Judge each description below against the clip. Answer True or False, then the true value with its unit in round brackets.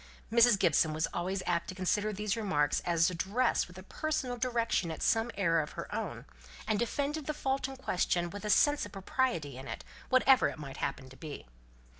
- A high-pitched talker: True (200 Hz)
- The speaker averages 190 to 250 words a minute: True (200 wpm)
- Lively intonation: True (6.7 semitones)